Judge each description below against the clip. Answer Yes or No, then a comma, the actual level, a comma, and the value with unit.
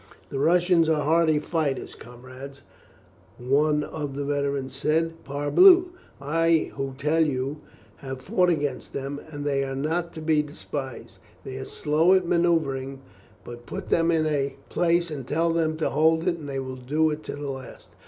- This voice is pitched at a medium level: Yes, medium, 150 Hz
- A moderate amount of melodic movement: Yes, average, 3.1 semitones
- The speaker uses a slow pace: No, average, 175 wpm